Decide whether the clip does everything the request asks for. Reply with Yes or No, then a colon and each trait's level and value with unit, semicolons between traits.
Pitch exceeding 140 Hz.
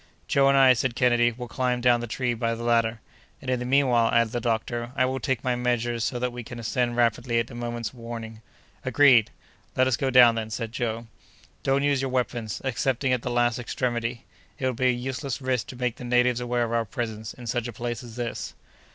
No: low, 120 Hz